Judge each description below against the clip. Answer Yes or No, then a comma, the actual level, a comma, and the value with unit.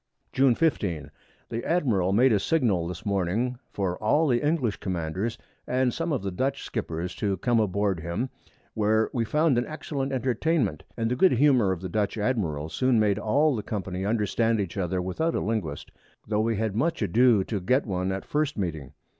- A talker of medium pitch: No, low, 110 Hz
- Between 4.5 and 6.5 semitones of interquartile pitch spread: Yes, average, 5.3 semitones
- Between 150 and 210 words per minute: Yes, average, 190 wpm